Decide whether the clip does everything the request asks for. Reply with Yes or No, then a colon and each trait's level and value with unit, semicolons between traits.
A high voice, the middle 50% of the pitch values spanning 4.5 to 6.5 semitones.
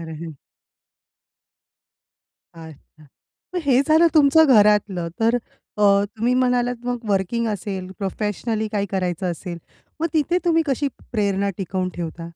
Yes: high, 210 Hz; average, 5.0 semitones